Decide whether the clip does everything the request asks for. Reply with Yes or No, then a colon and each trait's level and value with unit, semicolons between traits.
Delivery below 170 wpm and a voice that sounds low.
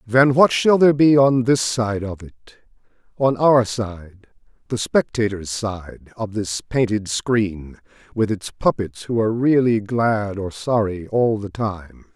Yes: average, 155 wpm; low, 110 Hz